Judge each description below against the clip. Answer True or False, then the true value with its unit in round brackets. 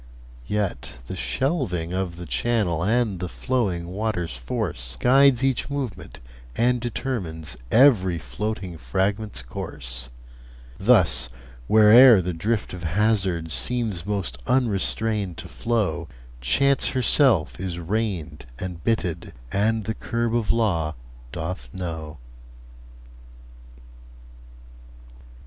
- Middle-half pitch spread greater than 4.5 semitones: True (5.5 semitones)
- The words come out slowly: True (105 wpm)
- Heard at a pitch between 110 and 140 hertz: False (95 Hz)